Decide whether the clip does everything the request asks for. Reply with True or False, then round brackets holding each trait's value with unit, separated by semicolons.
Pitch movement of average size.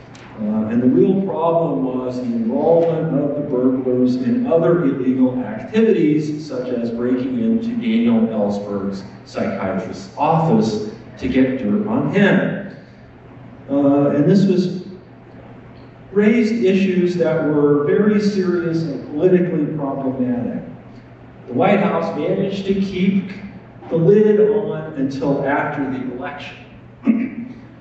False (7.1 semitones)